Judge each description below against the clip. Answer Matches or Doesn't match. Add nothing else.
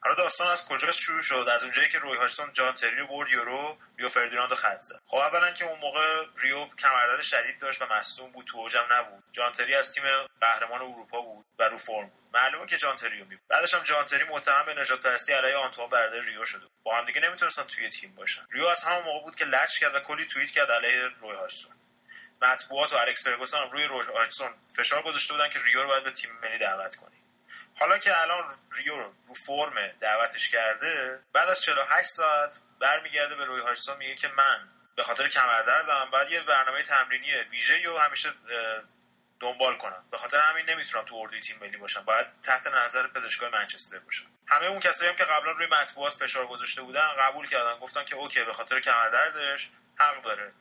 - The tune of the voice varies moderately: Matches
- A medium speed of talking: Doesn't match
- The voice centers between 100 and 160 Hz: Matches